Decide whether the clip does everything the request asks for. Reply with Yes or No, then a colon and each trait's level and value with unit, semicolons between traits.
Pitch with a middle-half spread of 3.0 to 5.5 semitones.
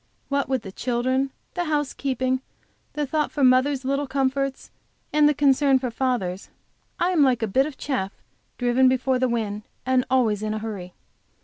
No: narrow, 2.5 semitones